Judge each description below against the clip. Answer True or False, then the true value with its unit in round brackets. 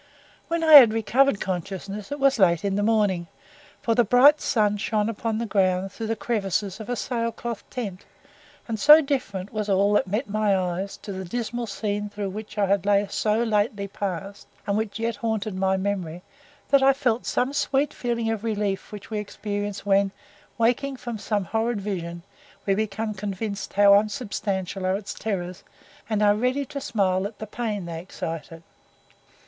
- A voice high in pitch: True (210 Hz)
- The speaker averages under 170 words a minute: False (175 wpm)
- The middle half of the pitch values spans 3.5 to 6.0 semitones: False (2.9 semitones)